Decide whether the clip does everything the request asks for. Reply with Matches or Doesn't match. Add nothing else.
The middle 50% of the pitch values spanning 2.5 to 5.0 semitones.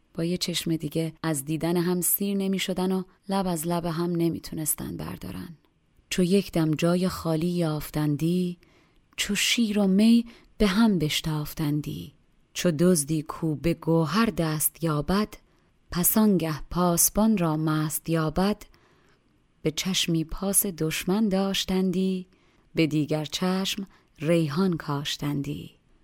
Matches